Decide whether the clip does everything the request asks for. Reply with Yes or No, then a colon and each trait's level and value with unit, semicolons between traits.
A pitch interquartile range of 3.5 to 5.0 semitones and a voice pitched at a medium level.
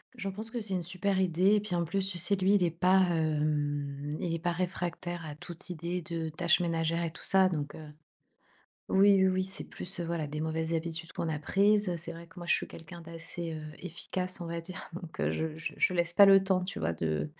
No: average, 2.7 semitones; medium, 170 Hz